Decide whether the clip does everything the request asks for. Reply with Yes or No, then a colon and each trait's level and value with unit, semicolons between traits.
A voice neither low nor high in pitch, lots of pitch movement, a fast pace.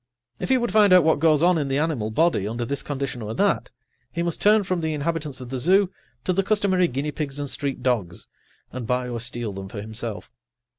Yes: medium, 145 Hz; wide, 6.2 semitones; fast, 230 wpm